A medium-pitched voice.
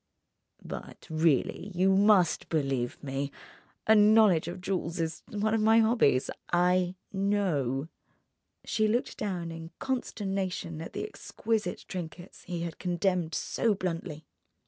Yes: medium, 180 Hz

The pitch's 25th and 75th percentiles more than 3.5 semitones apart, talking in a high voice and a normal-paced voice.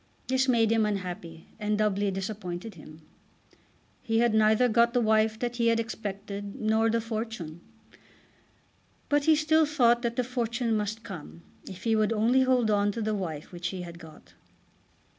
No: average, 3.1 semitones; high, 220 Hz; average, 170 wpm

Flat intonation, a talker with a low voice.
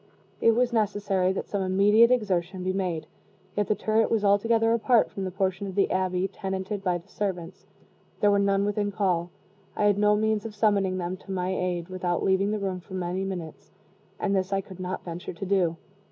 No: narrow, 2.0 semitones; high, 195 Hz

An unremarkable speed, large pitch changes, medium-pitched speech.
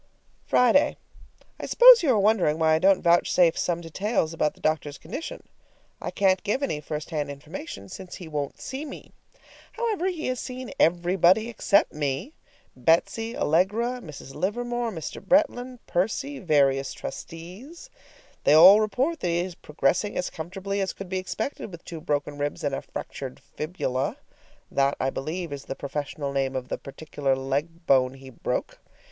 Yes: average, 165 wpm; wide, 6.9 semitones; medium, 170 Hz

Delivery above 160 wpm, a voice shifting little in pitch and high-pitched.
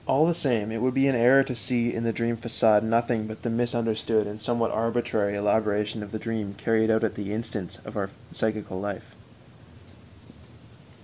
No: average, 185 wpm; narrow, 1.9 semitones; low, 115 Hz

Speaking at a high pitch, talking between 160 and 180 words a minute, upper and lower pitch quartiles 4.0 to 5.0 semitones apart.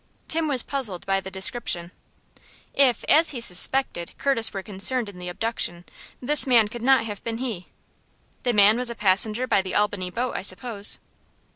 Yes: high, 225 Hz; average, 175 wpm; average, 4.7 semitones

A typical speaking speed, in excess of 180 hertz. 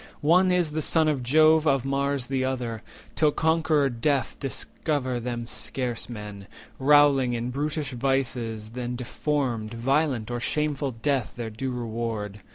No: average, 145 wpm; low, 130 Hz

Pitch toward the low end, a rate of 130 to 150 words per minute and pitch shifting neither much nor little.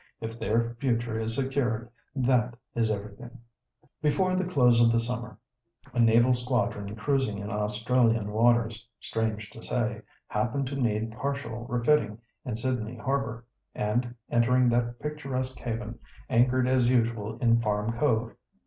No: low, 120 Hz; average, 140 wpm; narrow, 2.2 semitones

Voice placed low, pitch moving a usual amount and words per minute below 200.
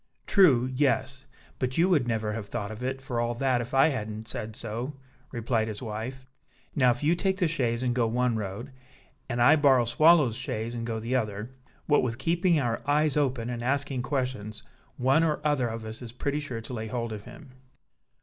No: low, 125 Hz; average, 3.5 semitones; fast, 205 wpm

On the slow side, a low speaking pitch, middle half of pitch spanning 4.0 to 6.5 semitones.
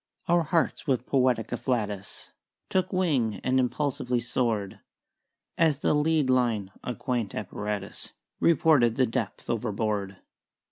Yes: slow, 120 wpm; low, 125 Hz; average, 5.2 semitones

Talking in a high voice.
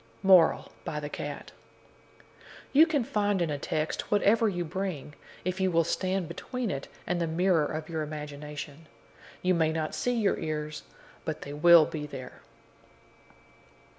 No: medium, 165 Hz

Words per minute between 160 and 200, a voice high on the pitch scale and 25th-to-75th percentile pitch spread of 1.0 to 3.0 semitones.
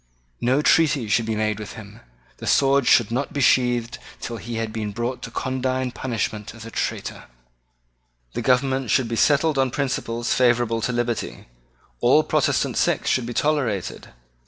No: average, 165 wpm; low, 120 Hz; narrow, 2.6 semitones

